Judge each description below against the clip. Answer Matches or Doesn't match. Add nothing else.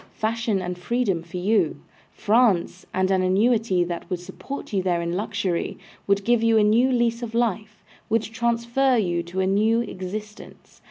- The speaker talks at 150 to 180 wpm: Matches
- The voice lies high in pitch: Matches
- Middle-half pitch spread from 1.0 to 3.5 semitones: Doesn't match